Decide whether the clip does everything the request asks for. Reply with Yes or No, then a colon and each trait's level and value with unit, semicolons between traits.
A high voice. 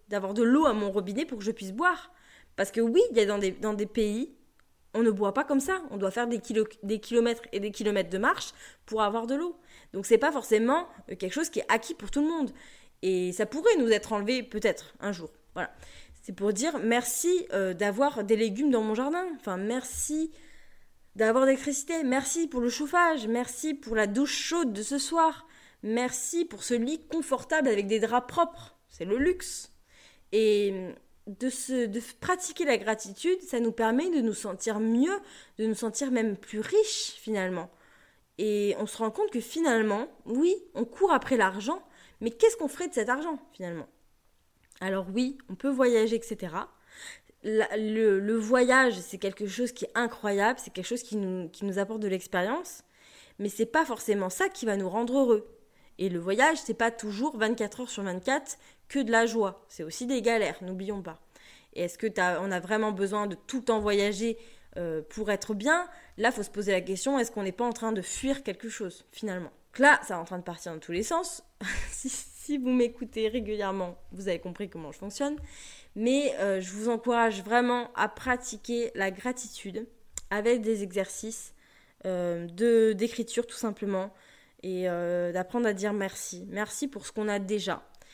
Yes: high, 225 Hz